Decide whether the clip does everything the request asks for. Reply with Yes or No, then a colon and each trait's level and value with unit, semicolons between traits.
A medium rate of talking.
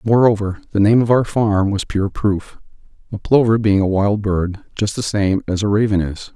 No: fast, 210 wpm